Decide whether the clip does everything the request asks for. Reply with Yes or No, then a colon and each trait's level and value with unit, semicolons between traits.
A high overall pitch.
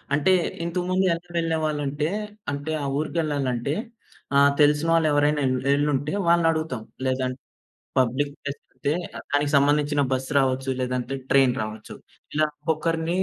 No: medium, 145 Hz